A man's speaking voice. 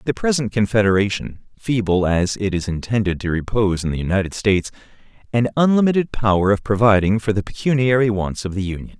Yes: male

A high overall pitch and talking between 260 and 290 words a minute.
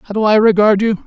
Yes: high, 210 Hz; fast, 280 wpm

